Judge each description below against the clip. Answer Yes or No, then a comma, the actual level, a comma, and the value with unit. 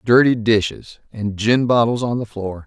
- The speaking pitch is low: Yes, low, 110 Hz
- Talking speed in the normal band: Yes, average, 180 wpm